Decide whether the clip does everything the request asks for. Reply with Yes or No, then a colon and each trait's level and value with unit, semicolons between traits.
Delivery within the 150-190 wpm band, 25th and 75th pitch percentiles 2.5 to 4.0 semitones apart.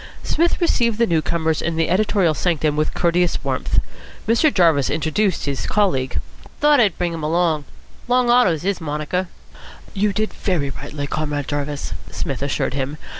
No: average, 160 wpm; wide, 5.6 semitones